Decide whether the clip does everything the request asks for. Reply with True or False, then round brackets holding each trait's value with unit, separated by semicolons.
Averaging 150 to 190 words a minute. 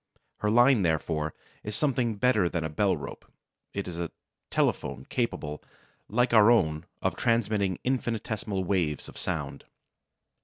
False (140 wpm)